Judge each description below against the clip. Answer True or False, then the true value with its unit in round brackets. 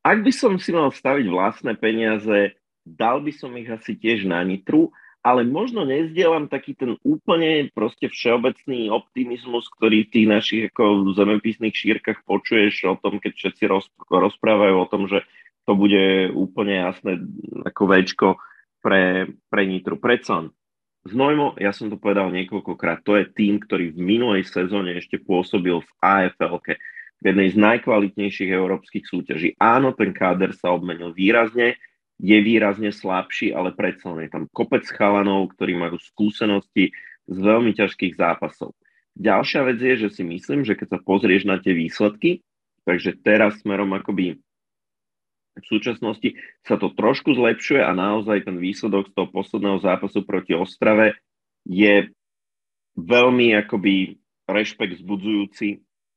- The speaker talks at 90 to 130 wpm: False (145 wpm)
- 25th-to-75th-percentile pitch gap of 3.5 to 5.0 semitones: False (2.8 semitones)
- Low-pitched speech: True (105 Hz)